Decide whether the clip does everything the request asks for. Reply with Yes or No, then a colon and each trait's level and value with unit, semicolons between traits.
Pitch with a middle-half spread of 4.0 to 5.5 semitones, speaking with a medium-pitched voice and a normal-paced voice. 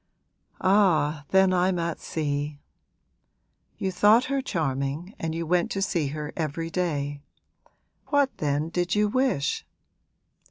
No: average, 4.4 semitones; medium, 170 Hz; slow, 125 wpm